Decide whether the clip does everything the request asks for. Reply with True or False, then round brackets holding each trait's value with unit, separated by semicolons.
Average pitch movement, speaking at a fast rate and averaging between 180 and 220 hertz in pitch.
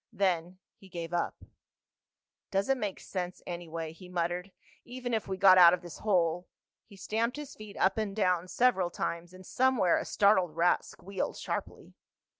False (3.1 semitones; 170 wpm; 185 Hz)